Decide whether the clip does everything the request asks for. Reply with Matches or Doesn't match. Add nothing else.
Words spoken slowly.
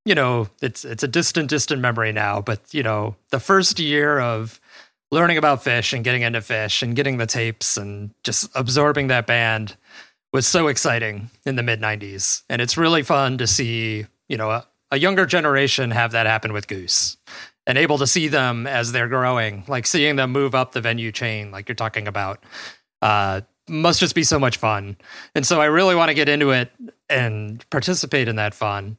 Doesn't match